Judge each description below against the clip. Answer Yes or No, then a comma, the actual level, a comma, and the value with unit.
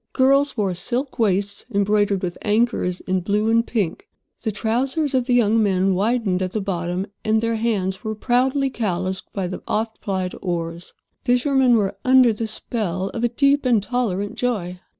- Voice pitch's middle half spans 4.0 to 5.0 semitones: Yes, average, 4.3 semitones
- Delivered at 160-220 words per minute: Yes, average, 170 wpm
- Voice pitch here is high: Yes, high, 215 Hz